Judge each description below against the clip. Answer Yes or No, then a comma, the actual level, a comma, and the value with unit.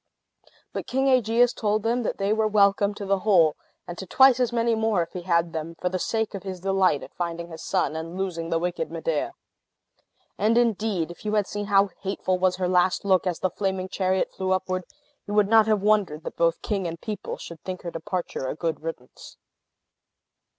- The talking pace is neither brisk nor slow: No, fast, 210 wpm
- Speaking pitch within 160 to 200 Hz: Yes, high, 190 Hz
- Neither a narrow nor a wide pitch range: Yes, average, 3.5 semitones